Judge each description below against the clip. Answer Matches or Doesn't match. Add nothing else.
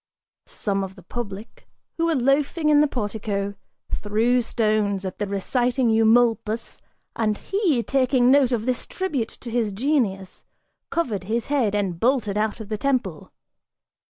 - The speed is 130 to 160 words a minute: Matches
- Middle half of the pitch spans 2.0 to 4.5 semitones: Matches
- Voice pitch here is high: Matches